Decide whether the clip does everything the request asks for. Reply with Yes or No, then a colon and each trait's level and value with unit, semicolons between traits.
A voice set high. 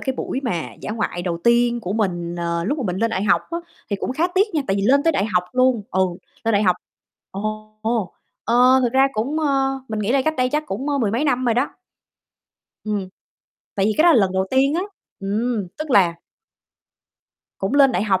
Yes: high, 230 Hz